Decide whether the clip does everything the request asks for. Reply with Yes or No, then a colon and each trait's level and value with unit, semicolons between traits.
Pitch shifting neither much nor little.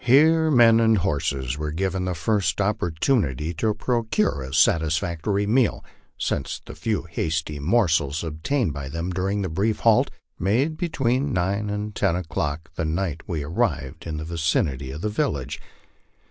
No: wide, 6.1 semitones